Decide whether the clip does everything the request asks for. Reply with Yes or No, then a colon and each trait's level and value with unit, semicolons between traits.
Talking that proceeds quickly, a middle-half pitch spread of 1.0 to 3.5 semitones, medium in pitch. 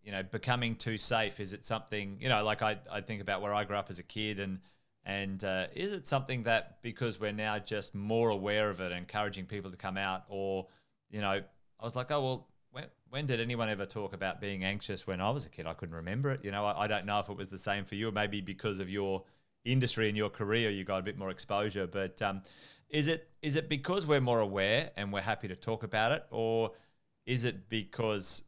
No: fast, 245 wpm; average, 2.7 semitones; low, 105 Hz